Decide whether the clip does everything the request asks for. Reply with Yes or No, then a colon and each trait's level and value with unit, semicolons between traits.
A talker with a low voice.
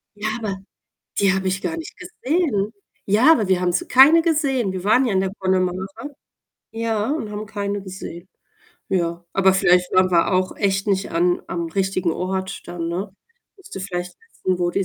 No: high, 195 Hz